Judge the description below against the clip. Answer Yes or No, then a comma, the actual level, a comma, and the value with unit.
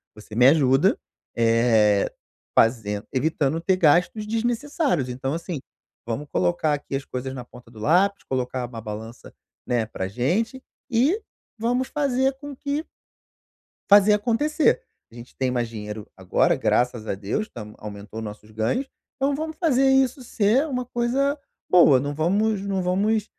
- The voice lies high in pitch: No, medium, 155 Hz